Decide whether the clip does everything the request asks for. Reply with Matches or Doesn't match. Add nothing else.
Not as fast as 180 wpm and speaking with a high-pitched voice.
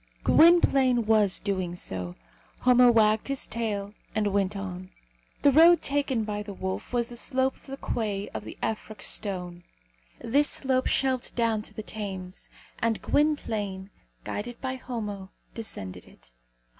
Matches